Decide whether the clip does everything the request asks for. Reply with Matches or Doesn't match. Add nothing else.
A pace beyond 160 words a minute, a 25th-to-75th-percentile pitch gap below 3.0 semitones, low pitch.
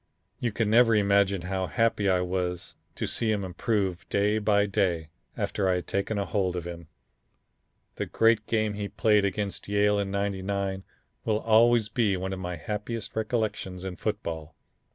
Matches